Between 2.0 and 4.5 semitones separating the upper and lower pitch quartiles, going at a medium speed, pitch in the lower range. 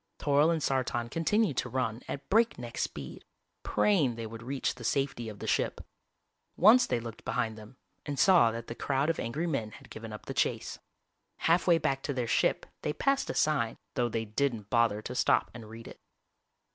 No: average, 4.9 semitones; average, 195 wpm; low, 125 Hz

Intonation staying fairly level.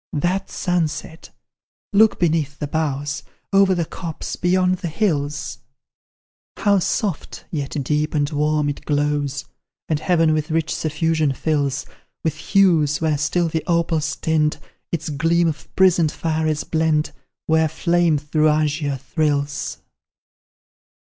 Yes: narrow, 2.3 semitones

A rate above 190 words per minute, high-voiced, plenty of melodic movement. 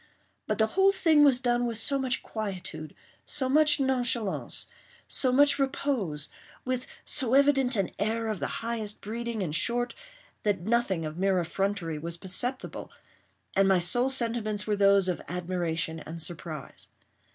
No: average, 140 wpm; high, 220 Hz; wide, 5.9 semitones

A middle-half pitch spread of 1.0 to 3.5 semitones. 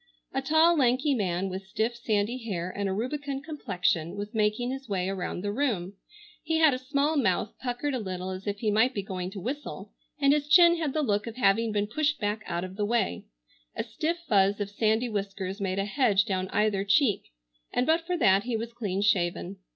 No: wide, 5.5 semitones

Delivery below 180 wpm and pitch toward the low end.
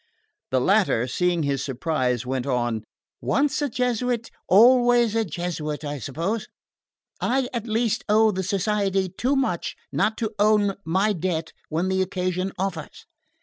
No: average, 145 wpm; high, 190 Hz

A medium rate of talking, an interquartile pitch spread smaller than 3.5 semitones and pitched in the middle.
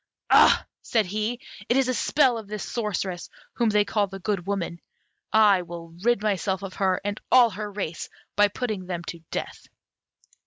No: average, 180 wpm; average, 2.7 semitones; high, 205 Hz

